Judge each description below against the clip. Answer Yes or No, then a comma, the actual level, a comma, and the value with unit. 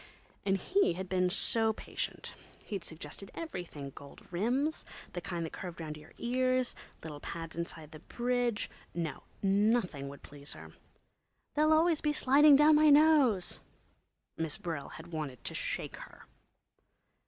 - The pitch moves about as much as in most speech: No, wide, 8.2 semitones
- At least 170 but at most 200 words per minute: No, average, 140 wpm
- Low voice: No, high, 190 Hz